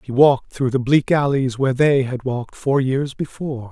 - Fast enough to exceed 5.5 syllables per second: No, 5.3 syllables/s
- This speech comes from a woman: No, male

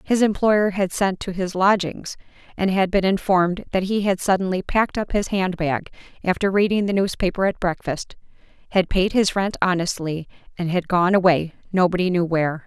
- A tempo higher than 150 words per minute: Yes, average, 180 wpm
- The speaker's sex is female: Yes, female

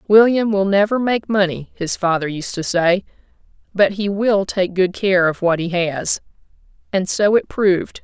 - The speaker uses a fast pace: No, average, 180 wpm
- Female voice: Yes, female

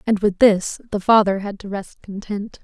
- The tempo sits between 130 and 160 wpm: No, fast, 205 wpm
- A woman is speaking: Yes, female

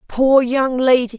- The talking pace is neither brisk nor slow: Yes, average, 150 wpm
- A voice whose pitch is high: Yes, very high, 255 Hz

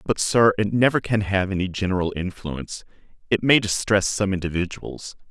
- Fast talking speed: No, average, 160 wpm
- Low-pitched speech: Yes, low, 100 Hz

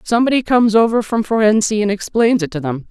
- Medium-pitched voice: No, high, 215 Hz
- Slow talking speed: No, fast, 205 wpm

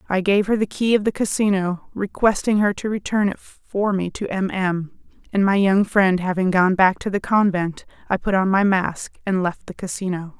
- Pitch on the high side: Yes, high, 195 Hz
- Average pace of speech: No, fast, 215 wpm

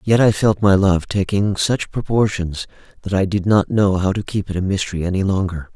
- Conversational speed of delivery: No, fast, 220 wpm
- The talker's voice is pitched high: No, very low, 95 Hz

